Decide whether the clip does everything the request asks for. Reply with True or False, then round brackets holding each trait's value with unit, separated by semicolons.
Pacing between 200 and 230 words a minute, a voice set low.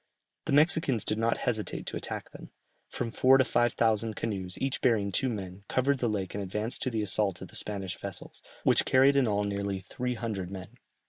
True (205 wpm; 110 Hz)